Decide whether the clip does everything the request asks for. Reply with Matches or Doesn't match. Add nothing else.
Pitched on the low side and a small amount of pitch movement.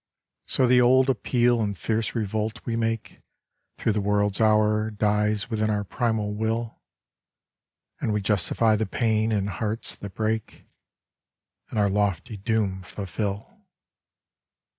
Matches